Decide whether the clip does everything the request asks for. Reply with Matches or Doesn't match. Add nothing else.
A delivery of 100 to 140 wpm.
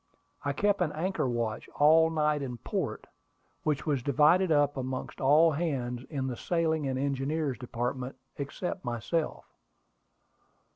Matches